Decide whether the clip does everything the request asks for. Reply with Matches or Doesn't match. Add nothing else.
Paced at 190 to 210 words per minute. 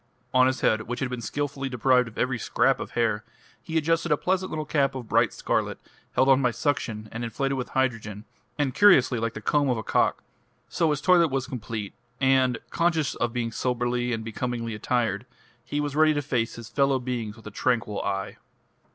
Matches